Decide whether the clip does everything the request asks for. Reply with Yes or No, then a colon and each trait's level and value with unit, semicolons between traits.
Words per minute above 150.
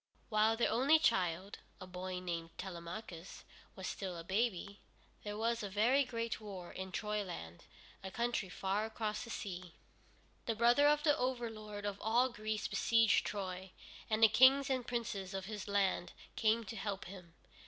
Yes: average, 165 wpm